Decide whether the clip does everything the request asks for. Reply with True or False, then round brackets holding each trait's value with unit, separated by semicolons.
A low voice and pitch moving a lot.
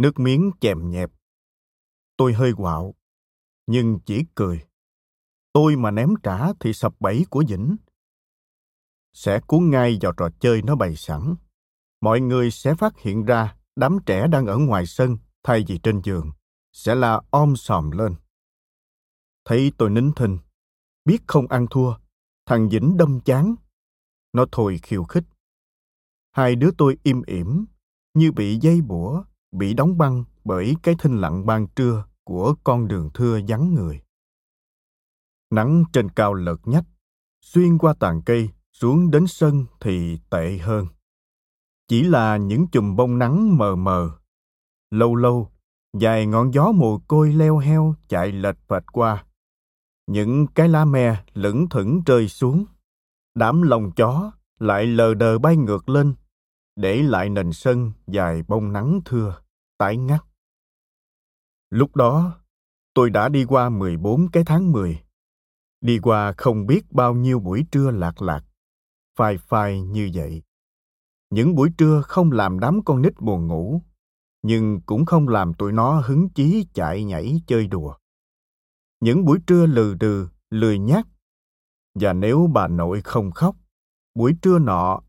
True (120 Hz; 7.0 semitones)